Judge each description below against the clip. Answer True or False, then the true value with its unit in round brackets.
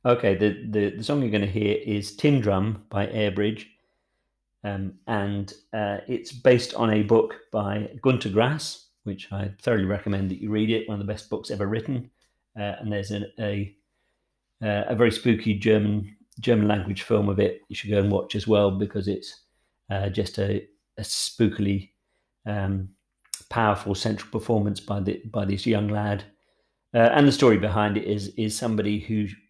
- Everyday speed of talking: True (180 wpm)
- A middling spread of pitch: False (1.8 semitones)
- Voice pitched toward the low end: True (105 Hz)